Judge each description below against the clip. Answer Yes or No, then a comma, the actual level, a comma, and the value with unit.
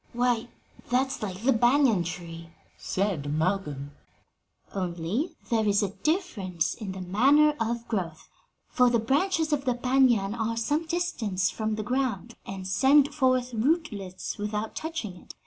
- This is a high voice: Yes, high, 225 Hz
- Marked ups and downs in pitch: Yes, wide, 5.8 semitones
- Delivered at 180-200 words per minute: No, average, 145 wpm